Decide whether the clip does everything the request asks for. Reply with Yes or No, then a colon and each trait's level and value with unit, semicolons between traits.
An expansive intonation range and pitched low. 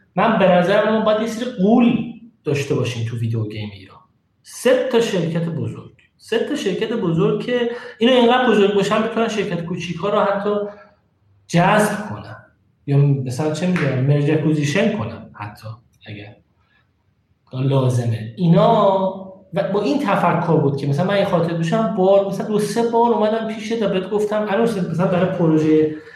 No: wide, 7.2 semitones; high, 190 Hz